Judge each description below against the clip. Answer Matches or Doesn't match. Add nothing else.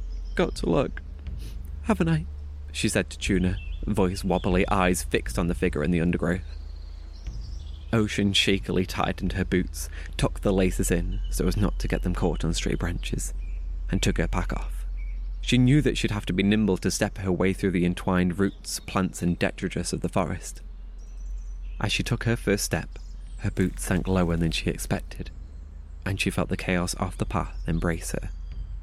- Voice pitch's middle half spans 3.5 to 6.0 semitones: Matches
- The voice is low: Matches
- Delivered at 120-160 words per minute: Doesn't match